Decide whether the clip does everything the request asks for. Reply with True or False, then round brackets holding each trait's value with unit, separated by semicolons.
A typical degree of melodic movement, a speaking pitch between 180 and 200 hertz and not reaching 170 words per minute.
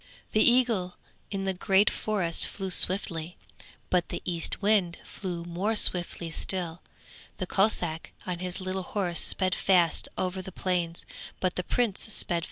False (2.1 semitones; 185 Hz; 155 wpm)